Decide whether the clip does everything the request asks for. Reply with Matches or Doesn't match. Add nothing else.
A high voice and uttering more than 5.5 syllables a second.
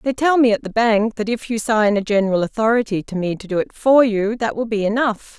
Matches